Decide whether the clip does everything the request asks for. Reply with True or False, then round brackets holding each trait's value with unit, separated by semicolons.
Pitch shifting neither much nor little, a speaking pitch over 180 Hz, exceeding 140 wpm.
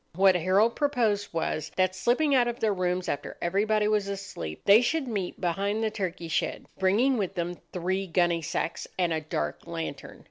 True (3.8 semitones; 190 Hz; 180 wpm)